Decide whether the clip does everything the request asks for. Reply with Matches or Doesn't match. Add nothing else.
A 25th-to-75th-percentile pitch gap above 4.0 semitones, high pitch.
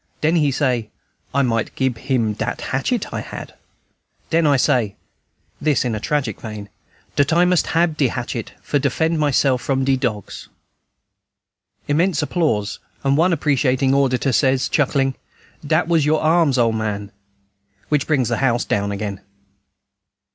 Doesn't match